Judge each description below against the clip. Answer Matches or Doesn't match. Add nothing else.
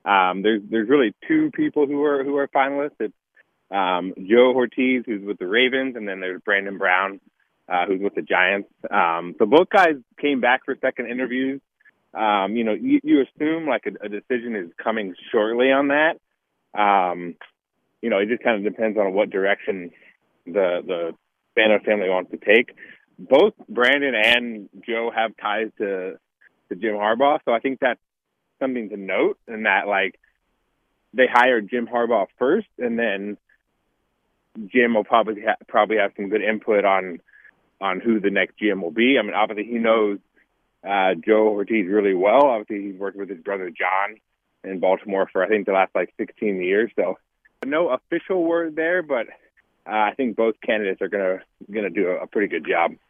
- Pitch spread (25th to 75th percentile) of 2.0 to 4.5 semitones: Doesn't match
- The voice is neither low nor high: Doesn't match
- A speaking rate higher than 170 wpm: Matches